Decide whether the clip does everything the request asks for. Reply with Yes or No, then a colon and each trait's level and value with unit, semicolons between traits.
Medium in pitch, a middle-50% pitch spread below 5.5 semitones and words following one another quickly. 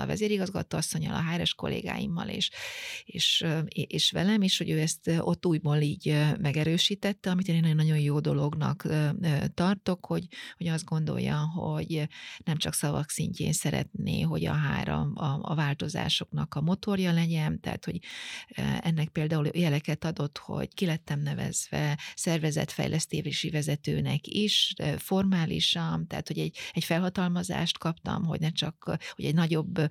No: medium, 160 Hz; average, 2.7 semitones; average, 140 wpm